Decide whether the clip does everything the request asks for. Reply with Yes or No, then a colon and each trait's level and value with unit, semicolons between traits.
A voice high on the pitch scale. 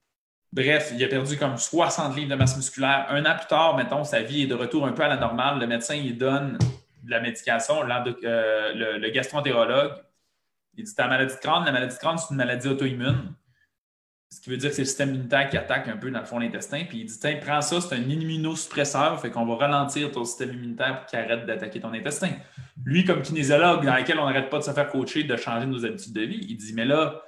No: low, 135 Hz